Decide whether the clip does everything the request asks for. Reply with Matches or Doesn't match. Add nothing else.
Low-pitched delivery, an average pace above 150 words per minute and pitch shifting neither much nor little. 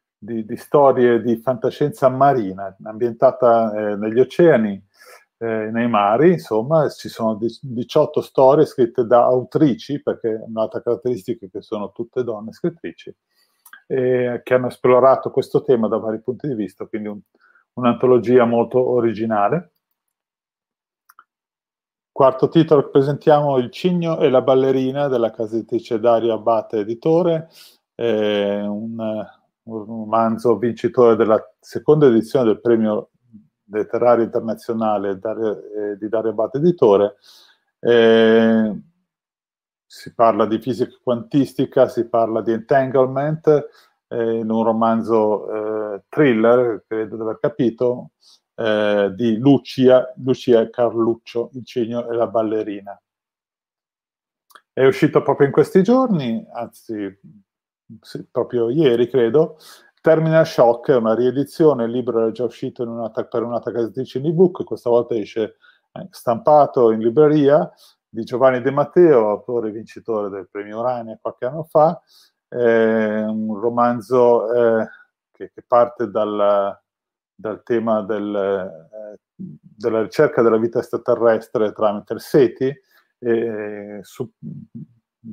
Doesn't match